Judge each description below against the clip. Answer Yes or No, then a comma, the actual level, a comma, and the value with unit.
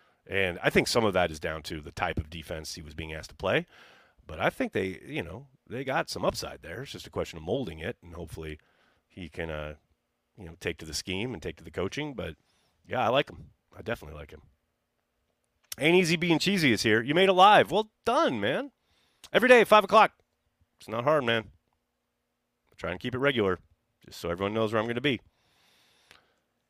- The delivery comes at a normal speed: No, fast, 220 wpm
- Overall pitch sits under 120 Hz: Yes, low, 105 Hz